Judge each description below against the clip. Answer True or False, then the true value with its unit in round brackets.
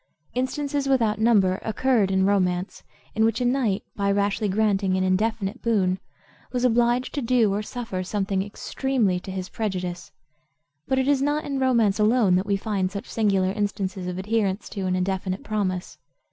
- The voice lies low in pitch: False (205 Hz)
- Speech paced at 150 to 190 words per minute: True (170 wpm)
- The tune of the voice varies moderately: True (3.8 semitones)